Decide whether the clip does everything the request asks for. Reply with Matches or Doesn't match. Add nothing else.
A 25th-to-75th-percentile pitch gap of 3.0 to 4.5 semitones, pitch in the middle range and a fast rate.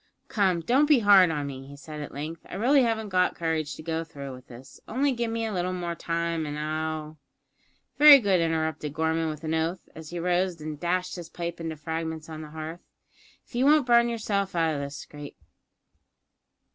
Matches